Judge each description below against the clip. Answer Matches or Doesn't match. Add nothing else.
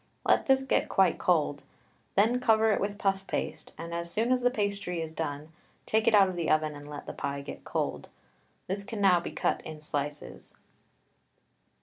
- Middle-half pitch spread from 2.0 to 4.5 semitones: Doesn't match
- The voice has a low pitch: Doesn't match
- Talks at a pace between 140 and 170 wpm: Doesn't match